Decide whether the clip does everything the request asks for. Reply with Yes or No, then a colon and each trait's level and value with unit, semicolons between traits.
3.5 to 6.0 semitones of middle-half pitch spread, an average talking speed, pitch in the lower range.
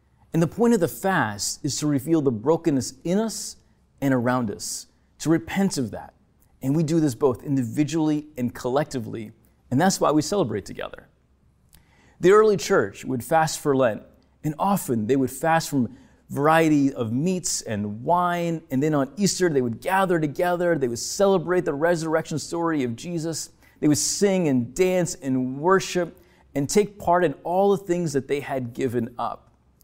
No: average, 5.2 semitones; average, 175 wpm; medium, 150 Hz